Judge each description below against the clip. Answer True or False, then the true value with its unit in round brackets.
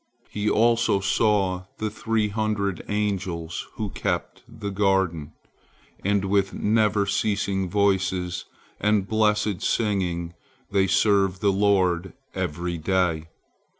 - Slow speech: True (110 wpm)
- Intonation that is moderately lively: False (2.3 semitones)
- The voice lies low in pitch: True (100 Hz)